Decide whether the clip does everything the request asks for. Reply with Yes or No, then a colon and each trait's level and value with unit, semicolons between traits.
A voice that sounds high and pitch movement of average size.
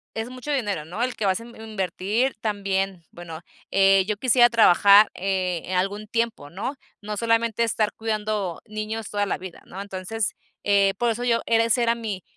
Yes: high, 210 Hz; average, 3.0 semitones